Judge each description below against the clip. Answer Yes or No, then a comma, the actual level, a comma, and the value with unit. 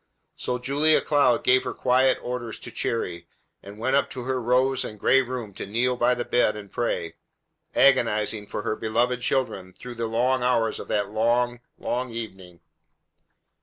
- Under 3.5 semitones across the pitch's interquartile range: Yes, average, 2.8 semitones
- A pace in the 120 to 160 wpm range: No, average, 170 wpm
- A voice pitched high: No, low, 120 Hz